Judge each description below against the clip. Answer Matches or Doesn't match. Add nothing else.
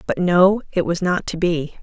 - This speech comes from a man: Doesn't match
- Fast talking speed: Matches